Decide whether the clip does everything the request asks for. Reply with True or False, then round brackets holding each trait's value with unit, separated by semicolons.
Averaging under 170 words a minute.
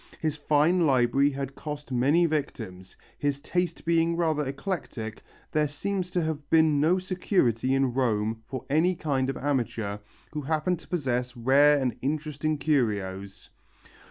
True (145 wpm)